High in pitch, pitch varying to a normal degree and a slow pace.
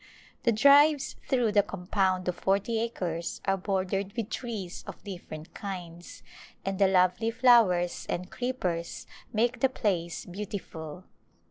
Yes: high, 195 Hz; average, 4.2 semitones; slow, 130 wpm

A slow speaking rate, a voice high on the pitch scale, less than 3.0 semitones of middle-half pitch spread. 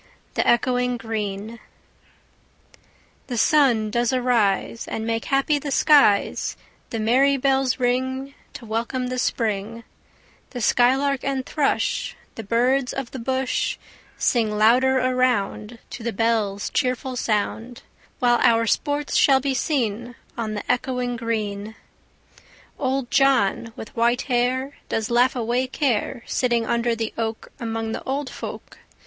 Yes: slow, 130 wpm; high, 245 Hz; narrow, 2.6 semitones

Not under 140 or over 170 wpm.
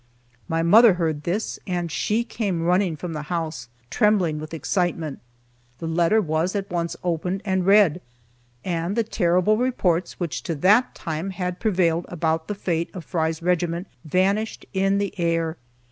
Yes: average, 160 wpm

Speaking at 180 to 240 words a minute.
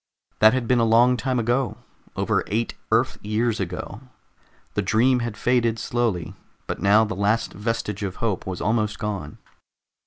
No: average, 160 wpm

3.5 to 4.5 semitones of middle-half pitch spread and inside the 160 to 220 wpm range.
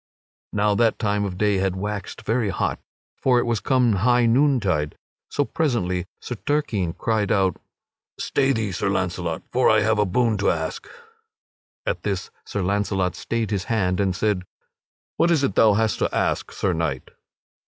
Yes: average, 3.9 semitones; average, 170 wpm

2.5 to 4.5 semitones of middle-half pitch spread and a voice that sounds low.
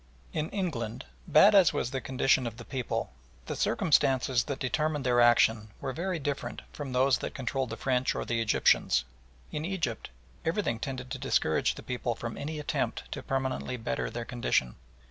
Yes: average, 3.8 semitones; low, 130 Hz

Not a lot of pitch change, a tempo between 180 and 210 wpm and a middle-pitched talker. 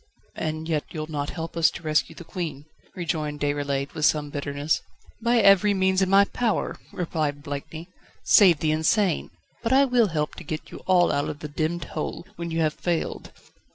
No: average, 3.7 semitones; average, 190 wpm; medium, 160 Hz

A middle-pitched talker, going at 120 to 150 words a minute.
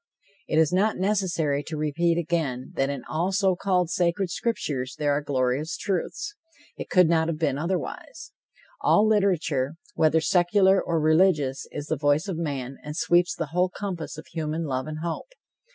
No: medium, 165 Hz; average, 170 wpm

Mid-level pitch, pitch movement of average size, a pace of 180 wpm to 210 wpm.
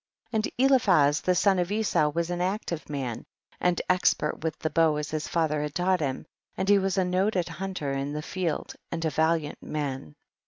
Yes: medium, 165 Hz; average, 3.9 semitones; average, 200 wpm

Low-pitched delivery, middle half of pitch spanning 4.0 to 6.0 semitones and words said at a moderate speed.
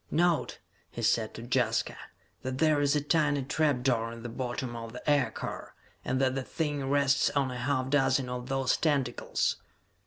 No: low, 130 Hz; average, 2.7 semitones; average, 180 wpm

